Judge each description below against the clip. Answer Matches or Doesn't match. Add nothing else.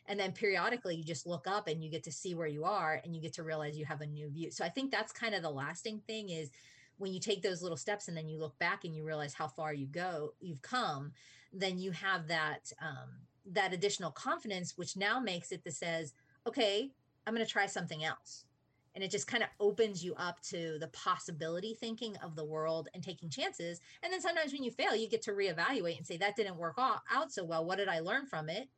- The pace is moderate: Doesn't match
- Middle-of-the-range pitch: Matches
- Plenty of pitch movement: Doesn't match